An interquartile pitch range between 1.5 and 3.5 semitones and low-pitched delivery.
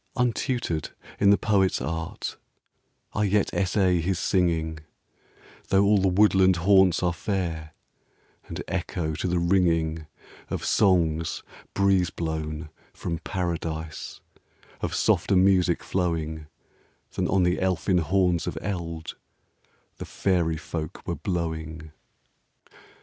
Yes: average, 3.0 semitones; very low, 90 Hz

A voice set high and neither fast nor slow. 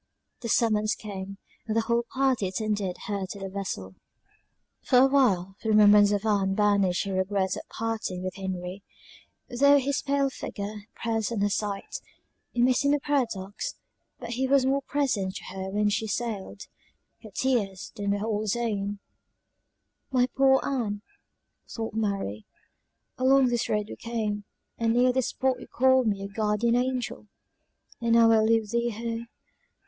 Yes: high, 220 Hz; average, 165 wpm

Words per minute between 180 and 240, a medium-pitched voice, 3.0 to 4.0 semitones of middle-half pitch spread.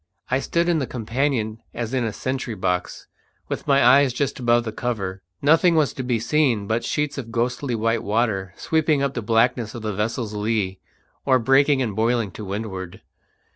No: average, 185 wpm; low, 120 Hz; average, 3.7 semitones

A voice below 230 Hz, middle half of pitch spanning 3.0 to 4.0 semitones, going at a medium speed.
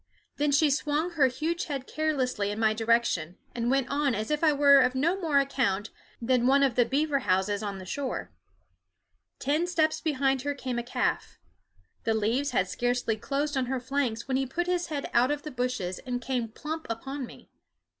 No: very high, 265 Hz; average, 3.7 semitones; average, 195 wpm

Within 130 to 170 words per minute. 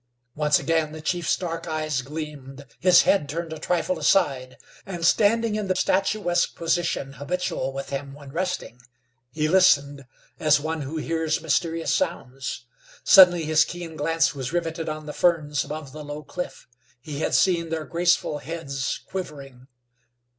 Yes: average, 155 wpm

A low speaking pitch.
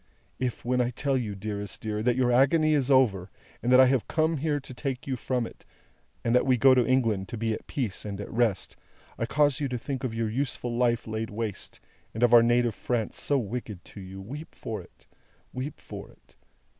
Yes: low, 120 Hz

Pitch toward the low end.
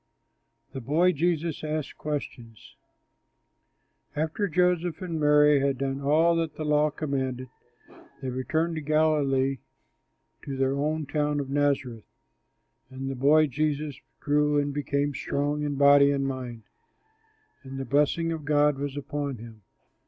No: medium, 145 Hz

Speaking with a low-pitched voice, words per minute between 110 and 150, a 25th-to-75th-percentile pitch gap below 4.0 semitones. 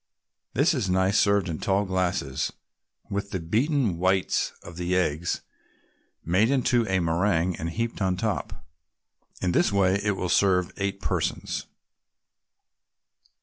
Yes: very low, 95 Hz; slow, 135 wpm; narrow, 2.6 semitones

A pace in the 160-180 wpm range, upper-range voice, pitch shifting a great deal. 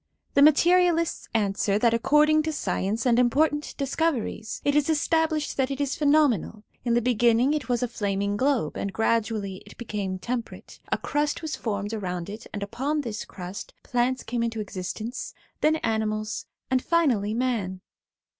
Yes: average, 170 wpm; high, 240 Hz; wide, 5.7 semitones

